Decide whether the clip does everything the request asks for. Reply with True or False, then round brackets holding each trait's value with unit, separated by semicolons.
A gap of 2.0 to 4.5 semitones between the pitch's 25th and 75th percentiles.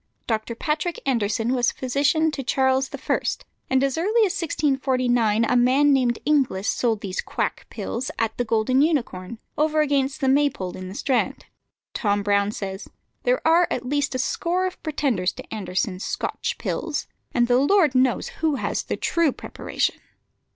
False (4.9 semitones)